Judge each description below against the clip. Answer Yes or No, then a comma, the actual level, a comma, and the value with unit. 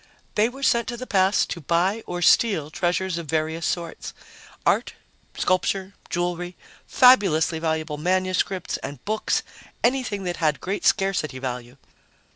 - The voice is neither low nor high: Yes, medium, 180 Hz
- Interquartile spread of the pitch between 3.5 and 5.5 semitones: Yes, average, 3.9 semitones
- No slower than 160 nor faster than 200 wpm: No, slow, 135 wpm